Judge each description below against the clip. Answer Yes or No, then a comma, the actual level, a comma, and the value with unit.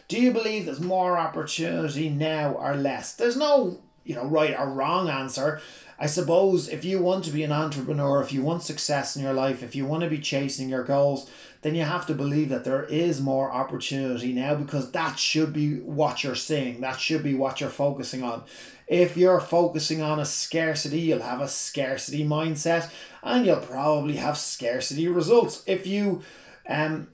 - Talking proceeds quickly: No, average, 190 wpm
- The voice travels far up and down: No, average, 3.1 semitones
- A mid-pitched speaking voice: Yes, medium, 150 Hz